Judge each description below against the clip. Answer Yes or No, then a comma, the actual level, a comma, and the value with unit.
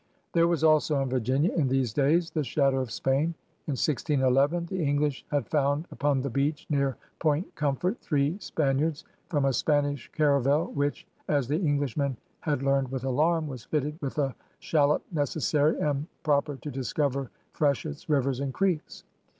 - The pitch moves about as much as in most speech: No, narrow, 2.1 semitones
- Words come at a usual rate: Yes, average, 175 wpm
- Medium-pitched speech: Yes, medium, 145 Hz